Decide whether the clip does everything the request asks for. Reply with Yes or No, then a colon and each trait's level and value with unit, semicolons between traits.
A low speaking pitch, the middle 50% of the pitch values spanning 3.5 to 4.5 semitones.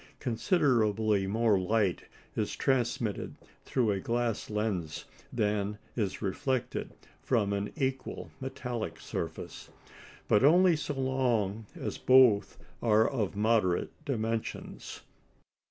Yes: low, 115 Hz; average, 3.9 semitones